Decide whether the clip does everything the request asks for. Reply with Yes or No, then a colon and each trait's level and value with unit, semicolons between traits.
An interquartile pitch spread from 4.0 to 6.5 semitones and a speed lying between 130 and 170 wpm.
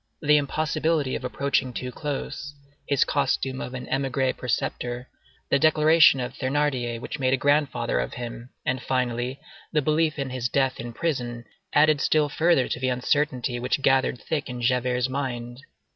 No: average, 2.9 semitones; average, 160 wpm